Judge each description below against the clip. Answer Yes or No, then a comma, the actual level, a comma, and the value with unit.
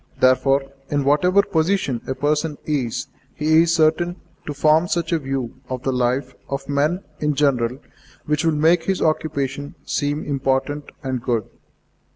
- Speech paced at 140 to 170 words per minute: Yes, average, 155 wpm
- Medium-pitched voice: Yes, medium, 145 Hz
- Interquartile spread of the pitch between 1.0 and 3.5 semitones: Yes, average, 3.0 semitones